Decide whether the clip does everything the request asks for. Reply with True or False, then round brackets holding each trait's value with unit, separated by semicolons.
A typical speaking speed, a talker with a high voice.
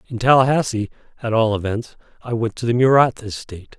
False (175 wpm; 115 Hz)